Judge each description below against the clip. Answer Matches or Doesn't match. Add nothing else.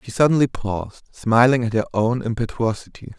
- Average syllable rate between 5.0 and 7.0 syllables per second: Matches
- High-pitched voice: Doesn't match